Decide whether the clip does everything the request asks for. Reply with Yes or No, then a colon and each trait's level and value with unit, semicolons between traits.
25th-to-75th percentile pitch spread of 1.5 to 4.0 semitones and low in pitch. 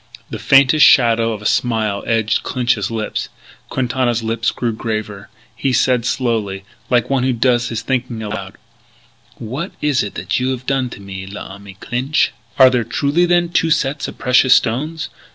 Yes: average, 3.2 semitones; low, 120 Hz